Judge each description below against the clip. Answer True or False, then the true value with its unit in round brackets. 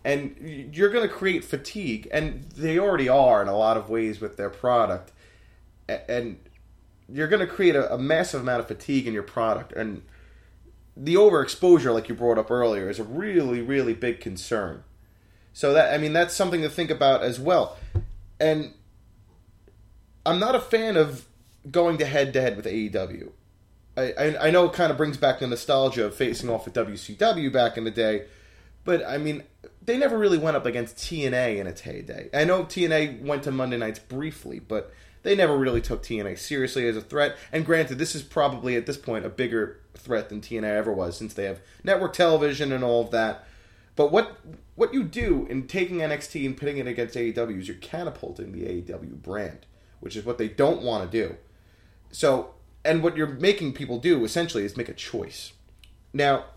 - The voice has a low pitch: True (125 Hz)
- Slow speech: False (195 wpm)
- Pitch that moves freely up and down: True (6.7 semitones)